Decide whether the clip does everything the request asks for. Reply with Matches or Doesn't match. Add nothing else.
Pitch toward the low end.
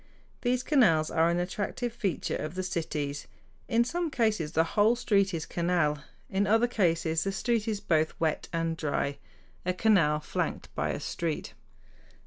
Doesn't match